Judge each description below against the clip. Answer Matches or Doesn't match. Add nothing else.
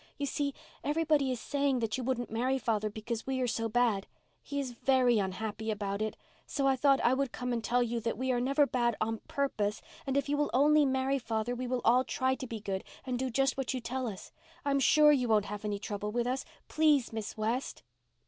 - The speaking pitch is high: Matches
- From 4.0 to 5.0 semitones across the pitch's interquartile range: Doesn't match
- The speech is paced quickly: Matches